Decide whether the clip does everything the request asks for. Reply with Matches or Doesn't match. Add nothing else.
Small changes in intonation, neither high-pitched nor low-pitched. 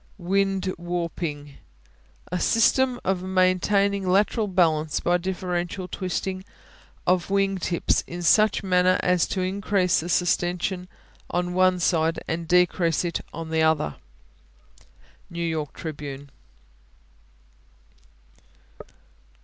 Matches